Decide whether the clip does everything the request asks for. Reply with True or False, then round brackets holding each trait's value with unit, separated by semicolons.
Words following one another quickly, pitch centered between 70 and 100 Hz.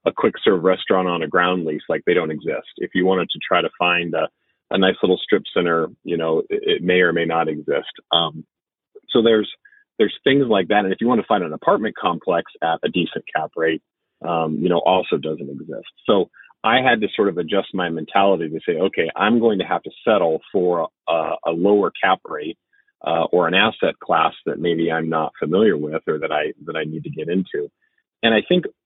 True (225 wpm; 95 Hz)